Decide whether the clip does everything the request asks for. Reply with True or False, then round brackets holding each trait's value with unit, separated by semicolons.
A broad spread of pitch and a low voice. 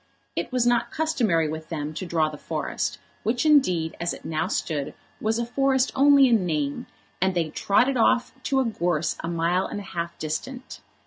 False (7.6 semitones; 185 Hz)